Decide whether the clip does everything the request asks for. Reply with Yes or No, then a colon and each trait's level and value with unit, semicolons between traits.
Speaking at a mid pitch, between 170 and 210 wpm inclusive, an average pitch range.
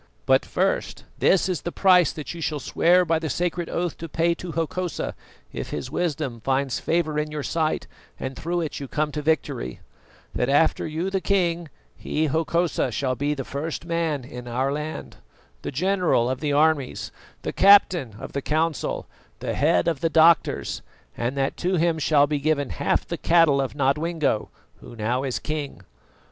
Yes: medium, 155 Hz; average, 180 wpm; average, 3.4 semitones